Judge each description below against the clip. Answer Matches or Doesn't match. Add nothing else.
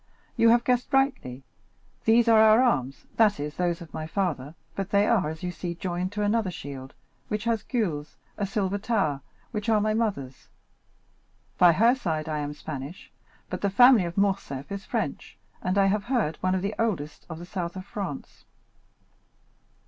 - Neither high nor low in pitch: Doesn't match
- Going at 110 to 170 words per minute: Doesn't match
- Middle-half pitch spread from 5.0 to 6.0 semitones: Matches